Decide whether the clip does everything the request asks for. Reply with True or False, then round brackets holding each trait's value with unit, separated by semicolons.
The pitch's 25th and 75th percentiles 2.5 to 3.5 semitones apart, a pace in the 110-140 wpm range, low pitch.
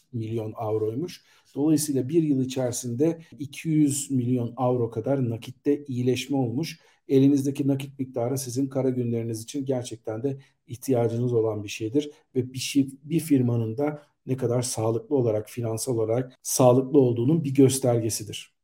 True (3.1 semitones; 135 wpm; 130 Hz)